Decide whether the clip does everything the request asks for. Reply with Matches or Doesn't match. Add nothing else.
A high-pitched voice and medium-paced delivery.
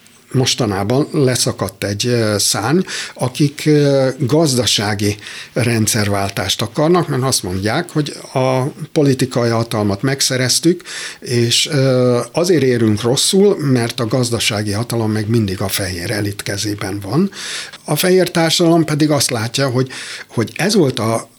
Doesn't match